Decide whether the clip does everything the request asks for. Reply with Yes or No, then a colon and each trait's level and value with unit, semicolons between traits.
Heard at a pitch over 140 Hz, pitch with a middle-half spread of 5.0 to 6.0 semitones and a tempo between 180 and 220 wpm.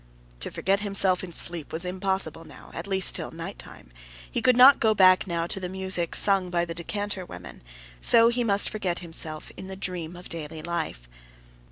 No: medium, 185 Hz; average, 2.8 semitones; average, 190 wpm